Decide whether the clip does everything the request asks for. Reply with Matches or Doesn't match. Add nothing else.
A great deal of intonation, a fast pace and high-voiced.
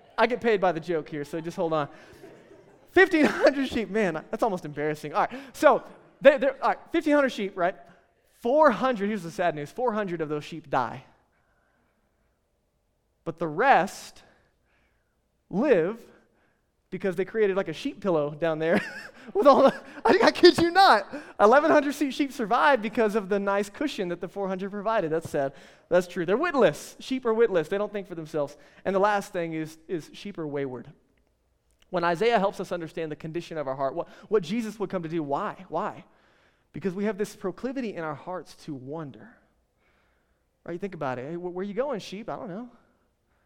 Doesn't match